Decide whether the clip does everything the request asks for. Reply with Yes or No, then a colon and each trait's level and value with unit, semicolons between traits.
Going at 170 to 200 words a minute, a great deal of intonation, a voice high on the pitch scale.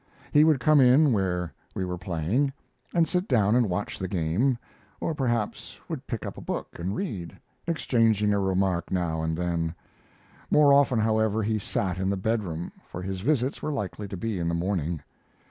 No: average, 185 wpm; wide, 5.8 semitones; low, 100 Hz